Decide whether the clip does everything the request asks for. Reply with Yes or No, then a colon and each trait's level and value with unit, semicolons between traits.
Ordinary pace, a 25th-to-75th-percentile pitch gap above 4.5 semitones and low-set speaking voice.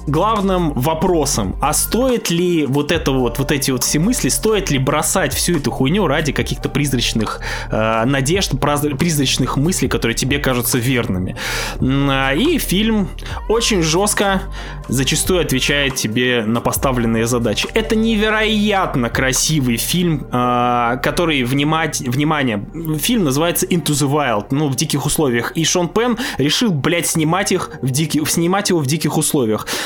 No: average, 145 wpm; average, 5.2 semitones; medium, 150 Hz